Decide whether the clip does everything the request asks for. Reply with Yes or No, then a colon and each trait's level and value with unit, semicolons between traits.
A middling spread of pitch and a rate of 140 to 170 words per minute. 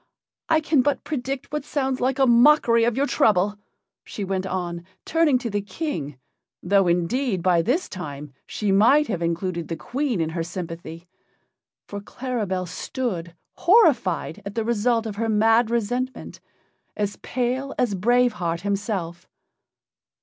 No: wide, 5.9 semitones; average, 150 wpm